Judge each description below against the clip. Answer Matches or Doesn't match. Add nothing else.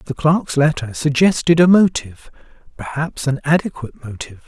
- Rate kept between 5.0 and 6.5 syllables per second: Matches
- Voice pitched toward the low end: Doesn't match